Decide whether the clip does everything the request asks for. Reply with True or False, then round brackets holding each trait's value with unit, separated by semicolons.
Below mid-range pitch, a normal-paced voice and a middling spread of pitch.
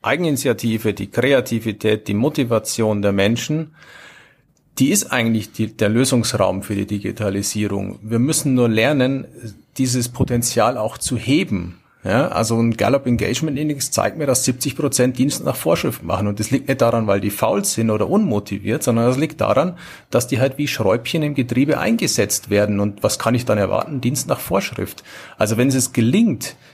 True (115 Hz; 170 wpm; 4.1 semitones)